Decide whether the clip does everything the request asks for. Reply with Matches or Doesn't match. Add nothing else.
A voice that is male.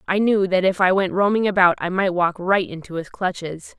Doesn't match